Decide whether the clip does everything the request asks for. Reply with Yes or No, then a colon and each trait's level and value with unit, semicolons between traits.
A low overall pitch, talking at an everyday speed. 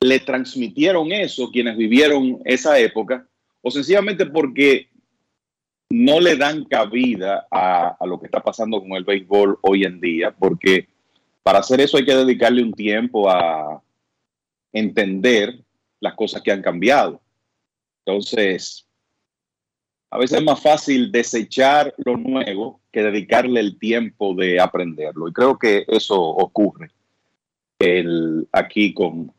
Yes: low, 120 Hz; average, 135 wpm